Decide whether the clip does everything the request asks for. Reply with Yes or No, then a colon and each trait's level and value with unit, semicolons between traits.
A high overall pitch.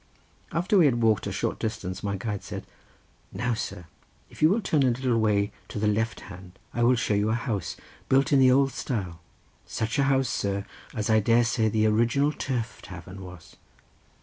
No: low, 110 Hz